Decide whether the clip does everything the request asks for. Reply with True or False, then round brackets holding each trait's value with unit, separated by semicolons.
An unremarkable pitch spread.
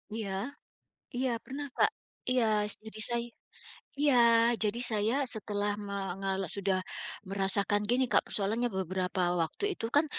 True (3.8 semitones)